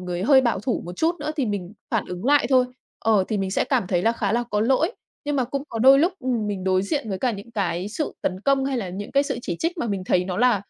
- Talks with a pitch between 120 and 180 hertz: No, high, 225 Hz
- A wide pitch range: Yes, wide, 6.0 semitones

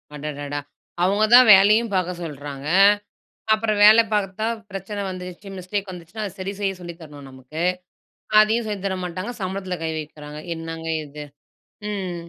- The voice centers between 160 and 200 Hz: Yes, medium, 185 Hz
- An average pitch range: Yes, average, 4.4 semitones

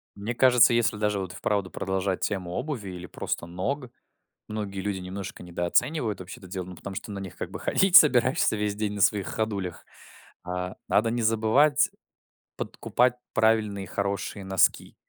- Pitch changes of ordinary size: Yes, average, 3.2 semitones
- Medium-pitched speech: No, low, 100 Hz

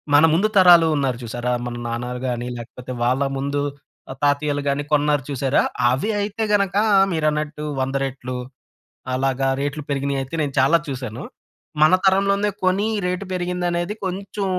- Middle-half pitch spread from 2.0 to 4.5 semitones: No, average, 5.3 semitones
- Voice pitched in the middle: Yes, medium, 145 Hz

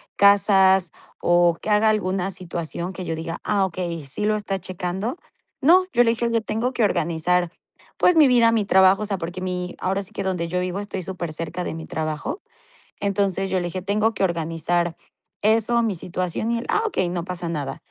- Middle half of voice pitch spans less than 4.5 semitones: Yes, average, 3.3 semitones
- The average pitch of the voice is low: No, medium, 185 Hz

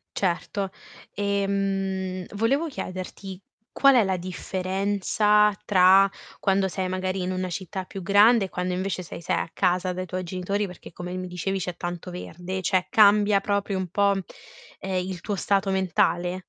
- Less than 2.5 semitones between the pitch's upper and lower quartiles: Yes, narrow, 1.6 semitones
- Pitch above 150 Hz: Yes, high, 190 Hz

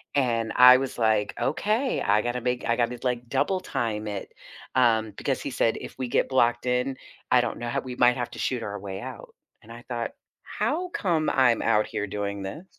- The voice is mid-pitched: No, low, 120 Hz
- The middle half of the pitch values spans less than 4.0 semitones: Yes, narrow, 2.6 semitones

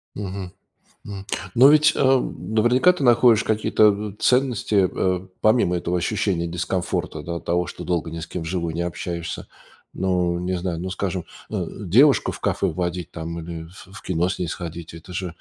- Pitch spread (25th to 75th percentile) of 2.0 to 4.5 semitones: Yes, average, 3.7 semitones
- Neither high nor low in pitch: No, very low, 90 Hz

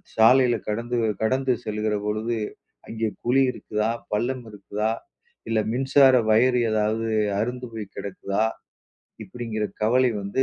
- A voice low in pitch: Yes, low, 115 Hz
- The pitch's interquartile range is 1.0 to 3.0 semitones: Yes, average, 2.7 semitones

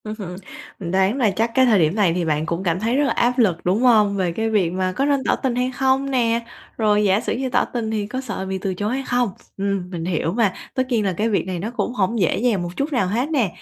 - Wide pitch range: No, average, 4.8 semitones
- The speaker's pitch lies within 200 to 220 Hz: Yes, high, 210 Hz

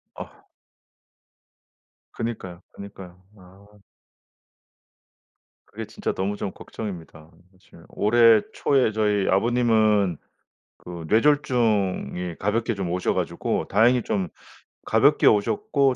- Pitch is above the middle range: No, low, 105 Hz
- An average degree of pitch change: Yes, average, 3.9 semitones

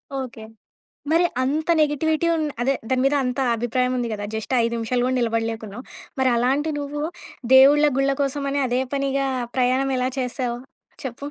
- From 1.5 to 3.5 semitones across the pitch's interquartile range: Yes, narrow, 2.5 semitones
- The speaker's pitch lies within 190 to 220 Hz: No, very high, 260 Hz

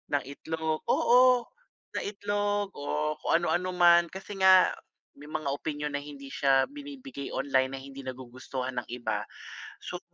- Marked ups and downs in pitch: Yes, wide, 6.1 semitones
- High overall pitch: No, medium, 150 Hz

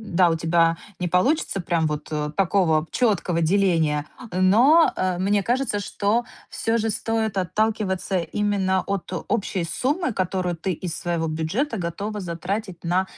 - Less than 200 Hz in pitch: Yes, medium, 185 Hz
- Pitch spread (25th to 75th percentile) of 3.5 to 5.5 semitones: Yes, average, 3.8 semitones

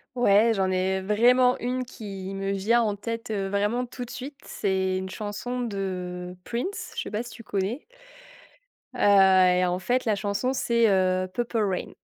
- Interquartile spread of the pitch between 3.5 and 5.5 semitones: Yes, average, 4.0 semitones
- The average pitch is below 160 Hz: No, high, 205 Hz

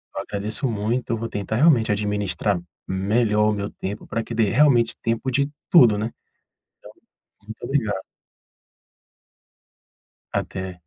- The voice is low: Yes, low, 110 Hz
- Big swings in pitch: No, narrow, 2.6 semitones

